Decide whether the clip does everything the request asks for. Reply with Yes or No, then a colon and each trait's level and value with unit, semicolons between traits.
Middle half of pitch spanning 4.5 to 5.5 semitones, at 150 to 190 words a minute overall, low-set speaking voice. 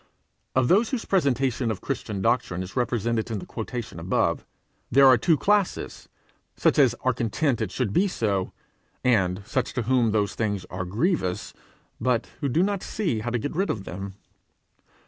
Yes: average, 5.1 semitones; average, 175 wpm; low, 120 Hz